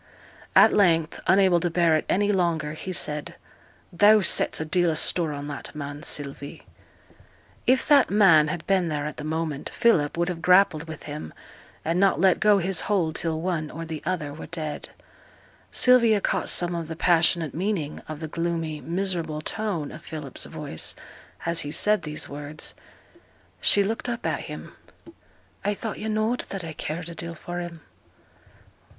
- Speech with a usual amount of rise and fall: Yes, average, 3.7 semitones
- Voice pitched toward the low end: No, medium, 170 Hz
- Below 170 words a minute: No, average, 175 wpm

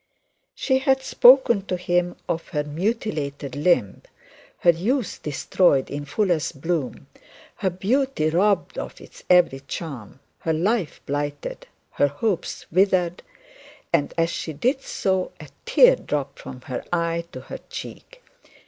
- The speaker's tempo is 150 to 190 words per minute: No, average, 140 wpm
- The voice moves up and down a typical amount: No, wide, 5.7 semitones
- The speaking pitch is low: No, medium, 170 Hz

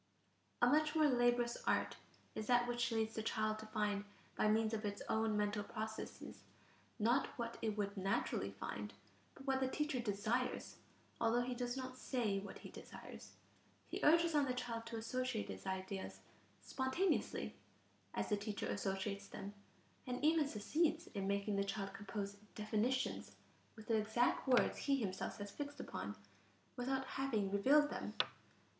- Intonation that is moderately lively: Yes, average, 3.8 semitones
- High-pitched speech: Yes, high, 225 Hz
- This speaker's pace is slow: No, average, 160 wpm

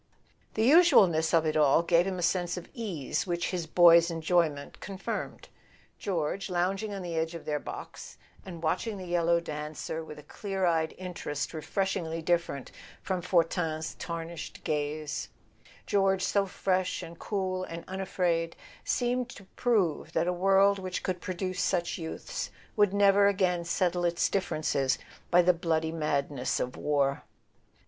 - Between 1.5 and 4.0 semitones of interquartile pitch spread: Yes, average, 2.9 semitones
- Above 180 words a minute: No, average, 155 wpm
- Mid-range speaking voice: Yes, medium, 175 Hz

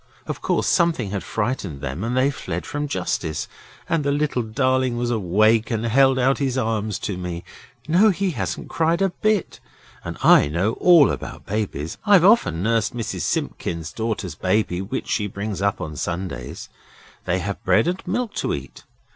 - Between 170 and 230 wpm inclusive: Yes, average, 180 wpm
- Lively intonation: Yes, wide, 7.3 semitones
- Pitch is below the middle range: Yes, low, 110 Hz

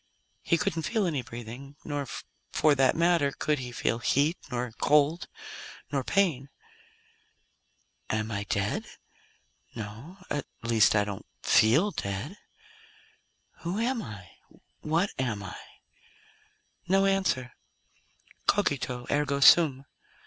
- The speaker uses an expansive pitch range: Yes, wide, 6.3 semitones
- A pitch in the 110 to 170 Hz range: Yes, medium, 140 Hz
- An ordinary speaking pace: No, slow, 115 wpm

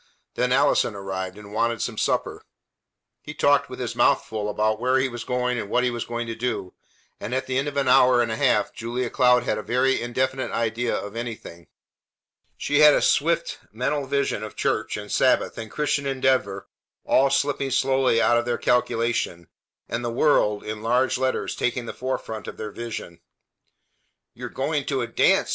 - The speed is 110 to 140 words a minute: No, average, 195 wpm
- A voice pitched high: No, low, 120 Hz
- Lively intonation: No, average, 3.2 semitones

